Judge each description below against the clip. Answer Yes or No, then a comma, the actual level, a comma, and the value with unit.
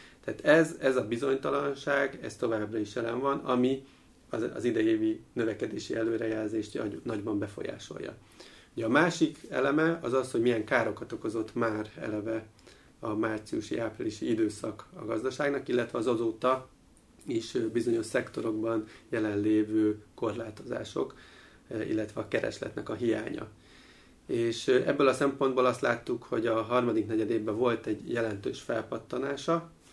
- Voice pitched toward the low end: Yes, low, 125 Hz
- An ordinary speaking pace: Yes, average, 125 wpm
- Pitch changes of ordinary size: Yes, average, 4.1 semitones